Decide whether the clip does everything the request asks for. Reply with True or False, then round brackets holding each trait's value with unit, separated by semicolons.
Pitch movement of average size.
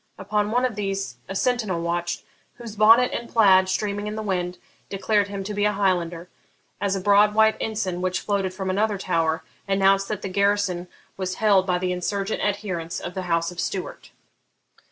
False (2.3 semitones)